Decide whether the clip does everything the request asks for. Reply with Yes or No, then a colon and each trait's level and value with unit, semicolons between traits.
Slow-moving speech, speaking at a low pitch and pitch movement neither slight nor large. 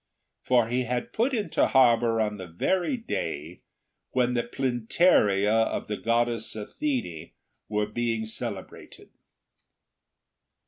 Yes: slow, 110 wpm; low, 115 Hz; average, 3.3 semitones